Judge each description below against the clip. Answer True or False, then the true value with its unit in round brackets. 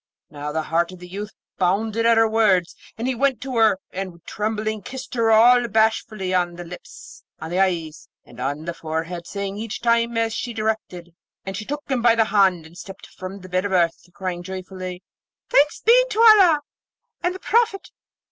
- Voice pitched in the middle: False (200 Hz)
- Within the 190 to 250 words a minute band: True (195 wpm)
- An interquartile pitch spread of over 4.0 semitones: True (4.5 semitones)